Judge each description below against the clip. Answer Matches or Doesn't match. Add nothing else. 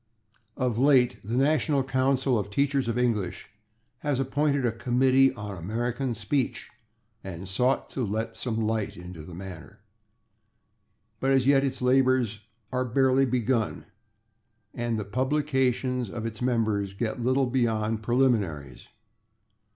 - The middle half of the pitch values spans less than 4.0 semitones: Matches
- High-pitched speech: Doesn't match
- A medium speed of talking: Doesn't match